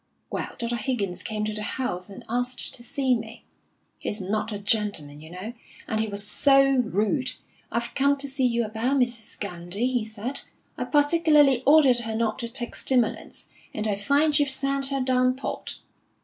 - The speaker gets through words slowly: No, average, 180 wpm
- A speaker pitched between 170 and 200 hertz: No, high, 240 Hz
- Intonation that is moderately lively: Yes, average, 4.0 semitones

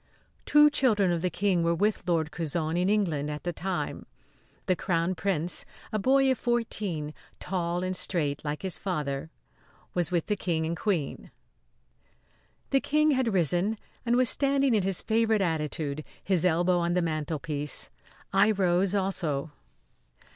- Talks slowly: No, average, 155 wpm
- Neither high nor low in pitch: Yes, medium, 180 Hz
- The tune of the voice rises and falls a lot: No, average, 4.2 semitones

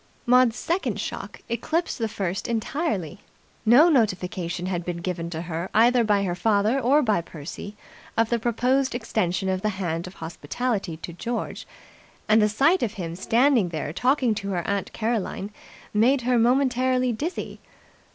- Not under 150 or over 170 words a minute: Yes, average, 160 wpm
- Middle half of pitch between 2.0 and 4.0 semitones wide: No, wide, 5.5 semitones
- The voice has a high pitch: Yes, high, 215 Hz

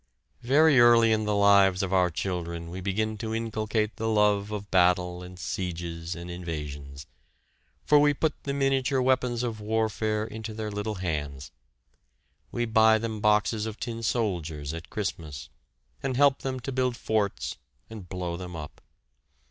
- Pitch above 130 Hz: No, low, 105 Hz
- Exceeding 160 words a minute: No, average, 155 wpm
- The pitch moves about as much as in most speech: Yes, average, 4.3 semitones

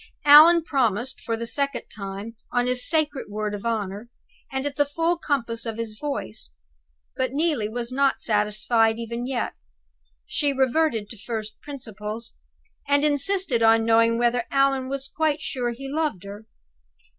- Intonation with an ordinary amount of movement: Yes, average, 4.1 semitones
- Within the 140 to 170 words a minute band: Yes, average, 155 wpm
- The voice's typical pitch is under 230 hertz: No, high, 245 Hz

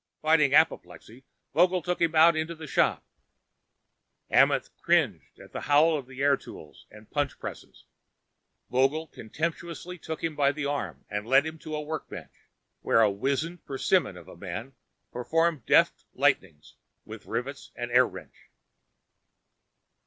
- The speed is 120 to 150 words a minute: Yes, average, 145 wpm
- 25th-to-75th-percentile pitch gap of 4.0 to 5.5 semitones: Yes, average, 4.8 semitones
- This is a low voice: No, medium, 145 Hz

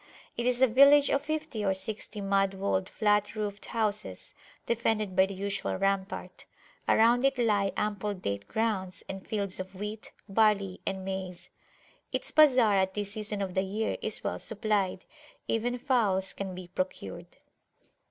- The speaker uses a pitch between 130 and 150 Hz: No, high, 205 Hz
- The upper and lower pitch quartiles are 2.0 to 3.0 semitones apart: Yes, average, 2.7 semitones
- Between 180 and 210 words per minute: No, average, 155 wpm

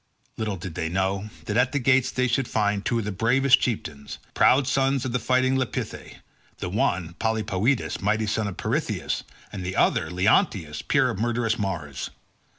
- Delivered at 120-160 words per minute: No, average, 170 wpm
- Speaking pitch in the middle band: No, low, 110 Hz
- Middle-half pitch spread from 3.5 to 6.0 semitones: Yes, average, 4.9 semitones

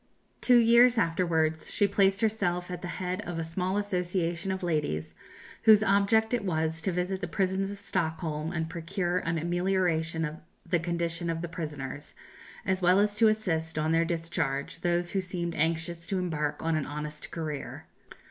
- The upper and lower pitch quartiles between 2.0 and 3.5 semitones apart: Yes, average, 2.9 semitones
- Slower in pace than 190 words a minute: Yes, average, 175 wpm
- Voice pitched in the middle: Yes, medium, 175 Hz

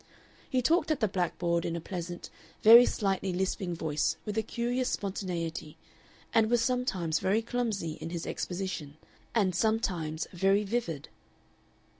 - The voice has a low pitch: No, high, 190 Hz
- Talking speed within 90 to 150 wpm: Yes, average, 140 wpm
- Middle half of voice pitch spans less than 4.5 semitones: No, average, 4.8 semitones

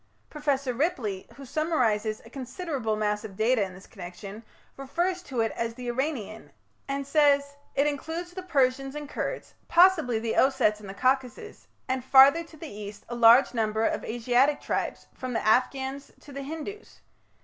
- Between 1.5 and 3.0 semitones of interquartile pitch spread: No, average, 4.6 semitones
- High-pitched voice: Yes, very high, 260 Hz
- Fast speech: No, average, 170 wpm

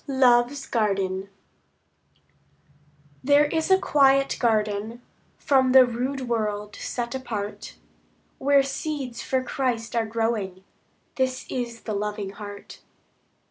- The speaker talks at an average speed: No, slow, 105 wpm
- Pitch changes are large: No, average, 4.0 semitones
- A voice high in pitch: Yes, high, 240 Hz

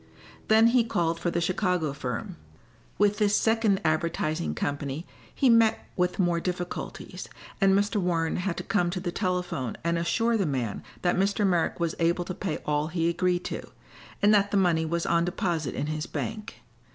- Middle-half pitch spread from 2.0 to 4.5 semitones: Yes, average, 3.5 semitones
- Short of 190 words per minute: Yes, average, 180 wpm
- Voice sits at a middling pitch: Yes, medium, 175 Hz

